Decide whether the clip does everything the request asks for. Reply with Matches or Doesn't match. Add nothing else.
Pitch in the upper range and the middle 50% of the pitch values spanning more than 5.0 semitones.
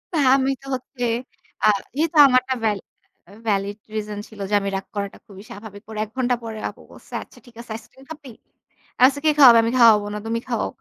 Doesn't match